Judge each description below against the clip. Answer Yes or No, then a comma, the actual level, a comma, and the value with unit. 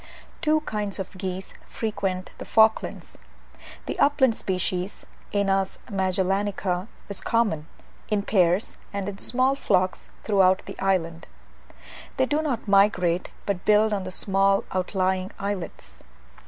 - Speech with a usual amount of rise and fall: No, narrow, 2.3 semitones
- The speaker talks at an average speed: No, slow, 125 wpm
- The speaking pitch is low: No, high, 195 Hz